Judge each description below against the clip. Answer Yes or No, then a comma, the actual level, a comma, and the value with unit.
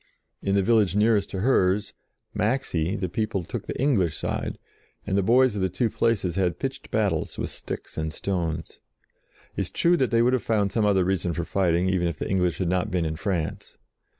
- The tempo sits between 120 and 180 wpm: No, fast, 205 wpm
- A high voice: No, very low, 95 Hz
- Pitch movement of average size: Yes, average, 3.7 semitones